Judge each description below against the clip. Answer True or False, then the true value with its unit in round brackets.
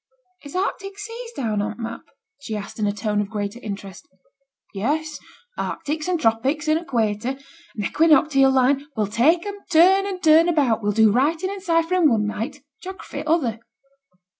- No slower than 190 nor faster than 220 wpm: False (180 wpm)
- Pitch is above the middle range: True (275 Hz)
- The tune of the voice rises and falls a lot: True (7.2 semitones)